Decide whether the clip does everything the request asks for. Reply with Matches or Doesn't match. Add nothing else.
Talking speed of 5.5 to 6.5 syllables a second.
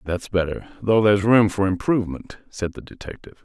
Matches